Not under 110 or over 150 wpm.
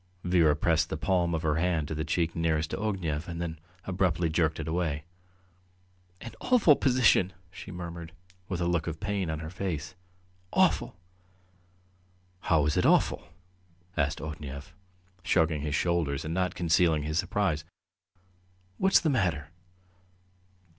Yes: average, 145 wpm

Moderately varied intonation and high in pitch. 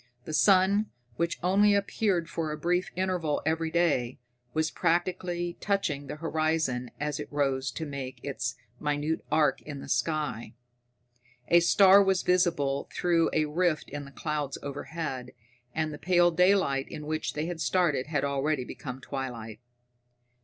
No: average, 3.8 semitones; medium, 155 Hz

